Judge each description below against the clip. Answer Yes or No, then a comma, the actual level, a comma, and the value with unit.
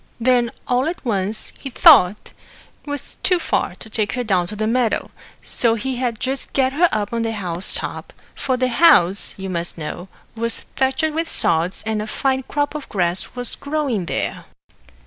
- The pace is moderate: Yes, average, 180 wpm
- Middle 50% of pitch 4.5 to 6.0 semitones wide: Yes, average, 4.9 semitones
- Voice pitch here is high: Yes, high, 230 Hz